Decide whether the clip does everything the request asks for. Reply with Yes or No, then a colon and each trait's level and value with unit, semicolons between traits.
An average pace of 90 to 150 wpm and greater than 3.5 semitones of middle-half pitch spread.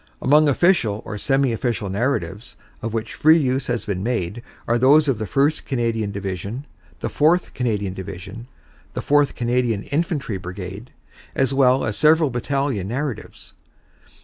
Yes: average, 145 wpm; average, 5.1 semitones